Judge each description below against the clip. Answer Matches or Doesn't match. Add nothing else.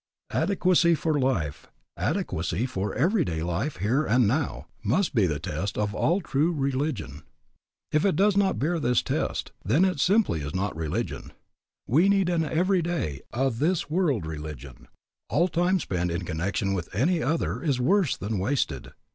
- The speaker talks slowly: Doesn't match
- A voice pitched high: Doesn't match